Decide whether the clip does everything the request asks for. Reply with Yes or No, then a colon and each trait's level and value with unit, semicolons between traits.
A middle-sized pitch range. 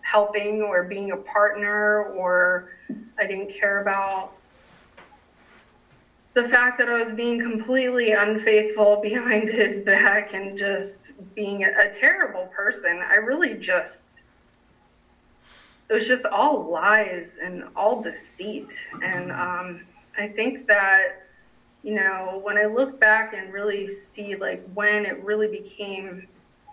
No: narrow, 2.0 semitones